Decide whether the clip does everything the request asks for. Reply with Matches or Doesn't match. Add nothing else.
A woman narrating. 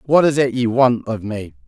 Doesn't match